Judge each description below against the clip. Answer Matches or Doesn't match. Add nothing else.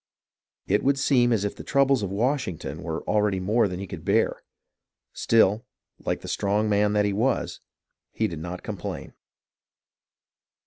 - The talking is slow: Doesn't match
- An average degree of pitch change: Matches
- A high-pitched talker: Doesn't match